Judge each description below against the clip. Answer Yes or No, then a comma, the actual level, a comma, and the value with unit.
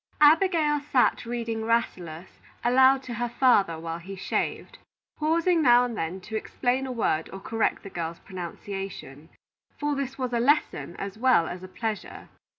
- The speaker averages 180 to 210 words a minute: No, average, 160 wpm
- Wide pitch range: Yes, wide, 6.0 semitones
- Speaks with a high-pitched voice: Yes, high, 230 Hz